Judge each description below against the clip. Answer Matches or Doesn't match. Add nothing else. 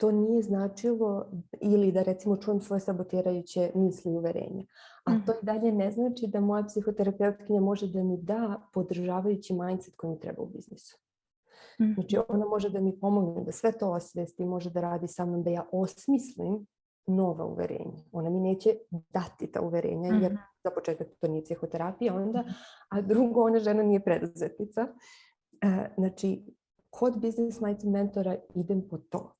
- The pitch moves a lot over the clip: Doesn't match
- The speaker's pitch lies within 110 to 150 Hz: Doesn't match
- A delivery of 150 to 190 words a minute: Matches